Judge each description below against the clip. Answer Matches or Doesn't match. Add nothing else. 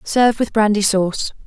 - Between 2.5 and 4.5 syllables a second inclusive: Doesn't match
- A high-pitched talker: Matches